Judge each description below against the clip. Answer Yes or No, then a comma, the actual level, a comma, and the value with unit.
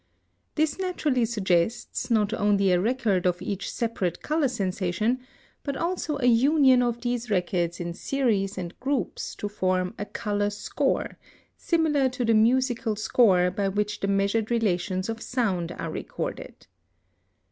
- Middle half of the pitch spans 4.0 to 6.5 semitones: Yes, average, 4.8 semitones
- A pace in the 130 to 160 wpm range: Yes, average, 145 wpm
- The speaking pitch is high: Yes, high, 215 Hz